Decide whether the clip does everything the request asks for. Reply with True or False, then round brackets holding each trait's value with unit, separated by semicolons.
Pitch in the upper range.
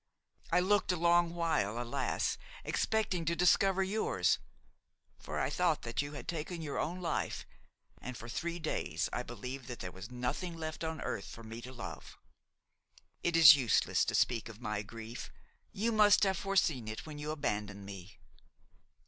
False (145 Hz)